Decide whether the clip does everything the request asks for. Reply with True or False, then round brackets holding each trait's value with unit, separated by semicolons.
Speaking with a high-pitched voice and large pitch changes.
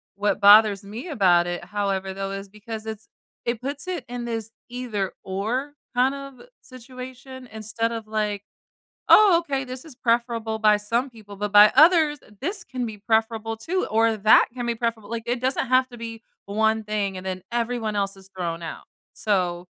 False (225 Hz; 3.6 semitones)